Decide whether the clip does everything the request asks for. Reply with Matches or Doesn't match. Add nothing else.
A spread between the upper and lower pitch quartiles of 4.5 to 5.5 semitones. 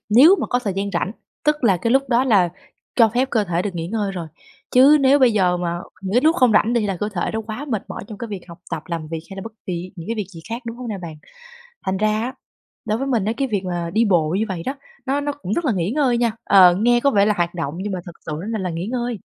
Matches